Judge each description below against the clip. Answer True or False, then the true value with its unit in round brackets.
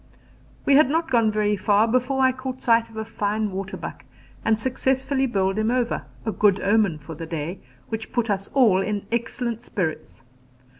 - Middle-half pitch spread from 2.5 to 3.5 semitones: False (4.0 semitones)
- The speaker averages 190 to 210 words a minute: False (180 wpm)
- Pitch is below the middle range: False (220 Hz)